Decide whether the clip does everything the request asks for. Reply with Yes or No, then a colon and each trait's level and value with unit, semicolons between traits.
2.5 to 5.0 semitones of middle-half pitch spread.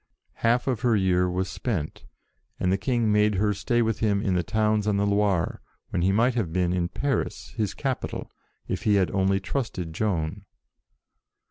Yes: average, 3.4 semitones